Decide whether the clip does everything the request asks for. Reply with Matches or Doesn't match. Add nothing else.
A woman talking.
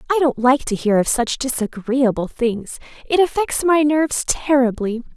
Matches